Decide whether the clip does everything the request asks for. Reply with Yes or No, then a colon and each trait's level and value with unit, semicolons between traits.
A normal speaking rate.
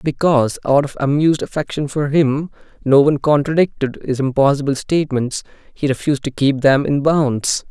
Yes: average, 155 wpm